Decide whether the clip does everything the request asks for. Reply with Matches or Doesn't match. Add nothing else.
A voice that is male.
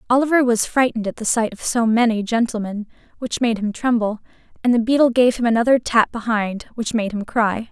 Doesn't match